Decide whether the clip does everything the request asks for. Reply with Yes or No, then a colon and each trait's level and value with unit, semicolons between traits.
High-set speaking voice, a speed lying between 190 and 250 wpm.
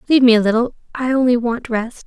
Yes: high, 240 Hz; fast, 205 wpm